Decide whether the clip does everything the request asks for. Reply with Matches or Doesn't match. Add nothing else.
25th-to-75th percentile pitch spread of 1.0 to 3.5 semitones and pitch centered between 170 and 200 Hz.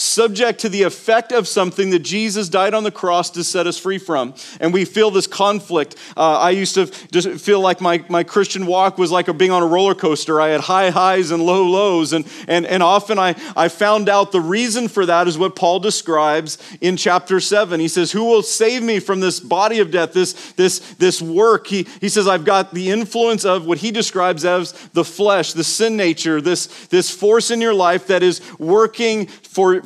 Matches